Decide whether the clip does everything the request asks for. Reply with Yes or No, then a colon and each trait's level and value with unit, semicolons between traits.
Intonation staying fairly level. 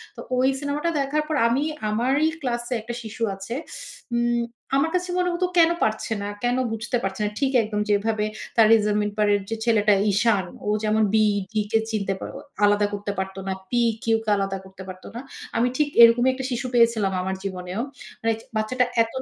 No: average, 3.4 semitones